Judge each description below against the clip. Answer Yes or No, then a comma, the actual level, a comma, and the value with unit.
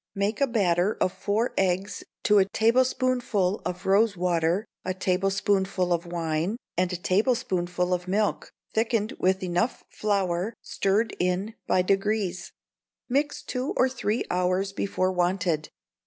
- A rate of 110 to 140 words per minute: Yes, slow, 135 wpm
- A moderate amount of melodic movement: Yes, average, 3.1 semitones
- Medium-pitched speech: No, high, 195 Hz